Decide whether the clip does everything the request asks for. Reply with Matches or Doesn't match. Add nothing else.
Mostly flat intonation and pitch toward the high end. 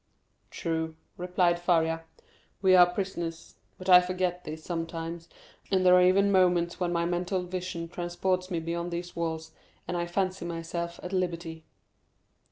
Doesn't match